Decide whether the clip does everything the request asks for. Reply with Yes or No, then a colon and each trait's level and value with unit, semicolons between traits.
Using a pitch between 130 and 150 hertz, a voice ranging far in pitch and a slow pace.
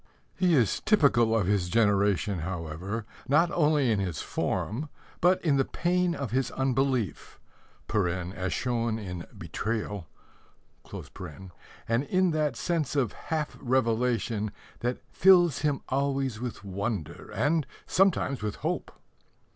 No: low, 120 Hz; wide, 6.3 semitones; slow, 125 wpm